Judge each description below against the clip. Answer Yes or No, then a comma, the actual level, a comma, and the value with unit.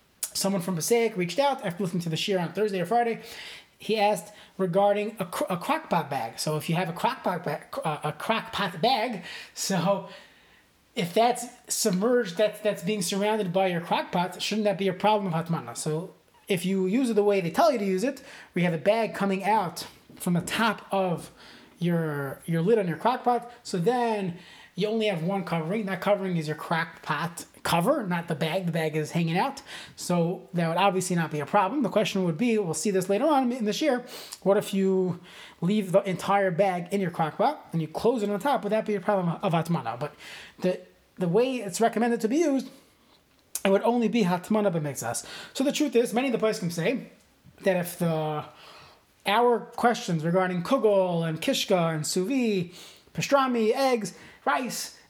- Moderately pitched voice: No, high, 195 Hz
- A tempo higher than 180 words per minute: Yes, average, 200 wpm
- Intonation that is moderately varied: Yes, average, 4.1 semitones